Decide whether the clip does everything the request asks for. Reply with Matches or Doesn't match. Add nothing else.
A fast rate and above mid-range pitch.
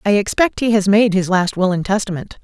Matches